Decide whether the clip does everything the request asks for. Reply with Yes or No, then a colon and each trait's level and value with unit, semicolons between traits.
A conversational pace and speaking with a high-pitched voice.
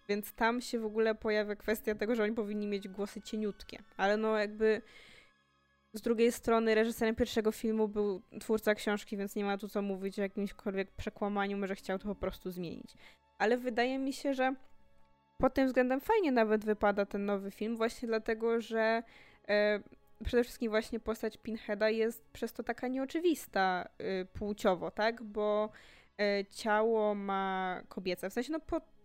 No: fast, 165 wpm; high, 215 Hz